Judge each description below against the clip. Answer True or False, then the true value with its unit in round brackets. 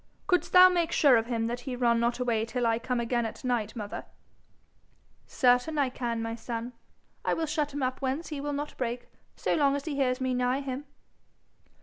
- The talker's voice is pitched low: False (250 Hz)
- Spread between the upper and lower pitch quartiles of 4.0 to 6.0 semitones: False (3.2 semitones)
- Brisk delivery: True (210 wpm)